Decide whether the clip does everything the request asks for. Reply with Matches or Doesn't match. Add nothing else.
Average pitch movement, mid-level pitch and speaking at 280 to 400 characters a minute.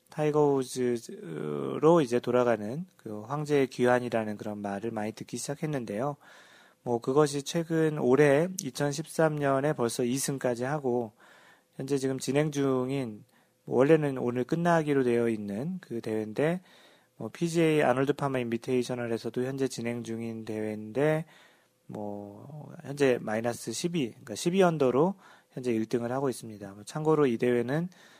Doesn't match